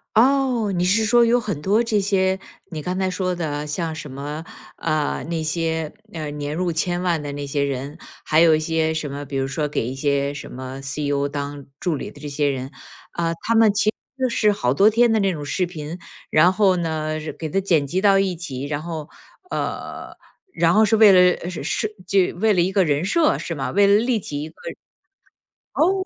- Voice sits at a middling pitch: Yes, medium, 165 Hz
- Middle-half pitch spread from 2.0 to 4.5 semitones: No, average, 5.0 semitones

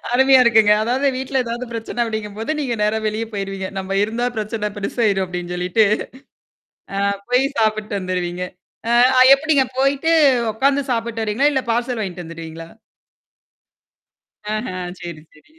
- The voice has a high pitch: Yes, high, 220 Hz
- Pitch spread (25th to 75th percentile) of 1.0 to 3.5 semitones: No, average, 4.4 semitones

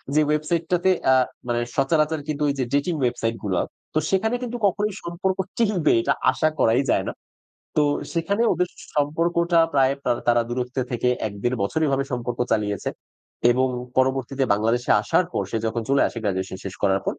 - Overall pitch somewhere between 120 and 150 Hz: Yes, low, 135 Hz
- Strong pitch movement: Yes, wide, 6.0 semitones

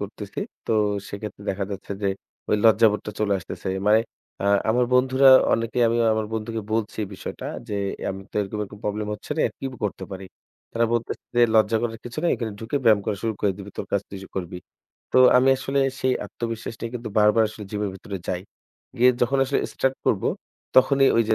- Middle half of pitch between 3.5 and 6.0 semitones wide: No, narrow, 2.6 semitones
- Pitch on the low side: Yes, low, 110 Hz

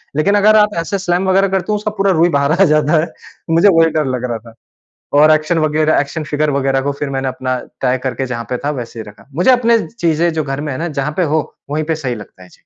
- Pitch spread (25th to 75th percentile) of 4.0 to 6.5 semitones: Yes, average, 4.3 semitones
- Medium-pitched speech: Yes, medium, 155 Hz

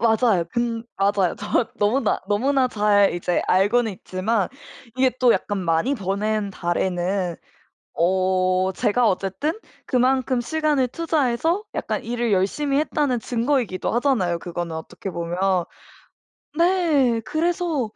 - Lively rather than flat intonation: Yes, wide, 5.7 semitones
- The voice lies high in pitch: Yes, high, 220 Hz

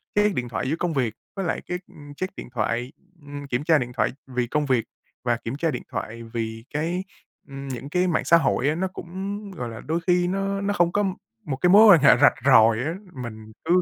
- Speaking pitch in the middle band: Yes, medium, 145 Hz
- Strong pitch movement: Yes, wide, 6.6 semitones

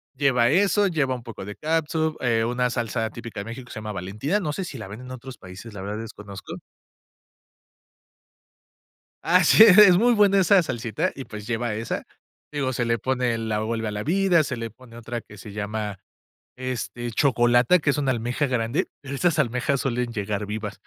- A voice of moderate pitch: No, low, 120 Hz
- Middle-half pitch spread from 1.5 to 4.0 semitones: No, average, 4.8 semitones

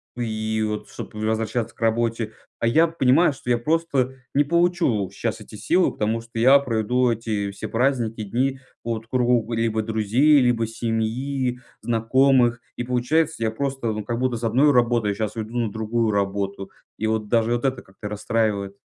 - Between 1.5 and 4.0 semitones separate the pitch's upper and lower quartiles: Yes, average, 2.7 semitones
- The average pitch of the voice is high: No, low, 115 Hz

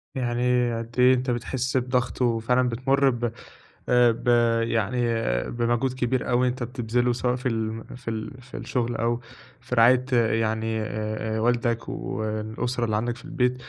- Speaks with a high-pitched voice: No, low, 120 Hz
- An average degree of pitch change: No, narrow, 1.7 semitones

